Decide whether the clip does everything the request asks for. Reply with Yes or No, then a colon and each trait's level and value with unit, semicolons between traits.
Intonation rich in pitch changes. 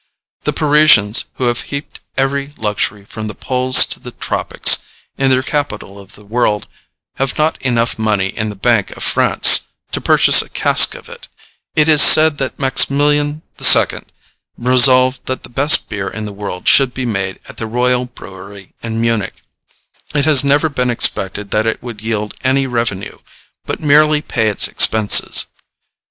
No: average, 4.6 semitones